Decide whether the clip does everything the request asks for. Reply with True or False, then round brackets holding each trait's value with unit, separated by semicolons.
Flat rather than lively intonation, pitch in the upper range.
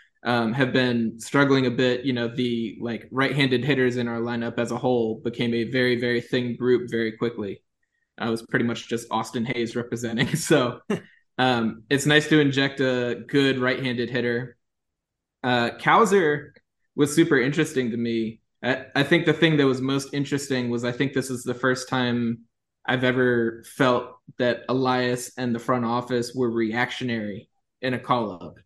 False (1.8 semitones; 125 Hz)